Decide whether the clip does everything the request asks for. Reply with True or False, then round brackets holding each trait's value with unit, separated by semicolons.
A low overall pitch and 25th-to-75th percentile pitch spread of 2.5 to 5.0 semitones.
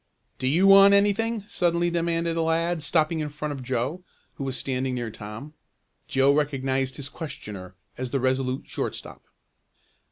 False (145 Hz; 4.6 semitones)